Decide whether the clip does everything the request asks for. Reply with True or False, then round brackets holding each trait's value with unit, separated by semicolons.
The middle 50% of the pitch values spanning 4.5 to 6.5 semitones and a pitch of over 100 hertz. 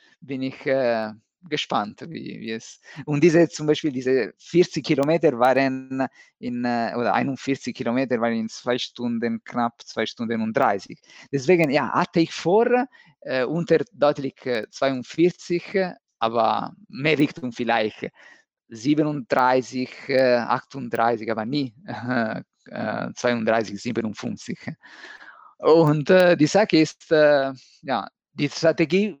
True (4.8 semitones; 135 Hz)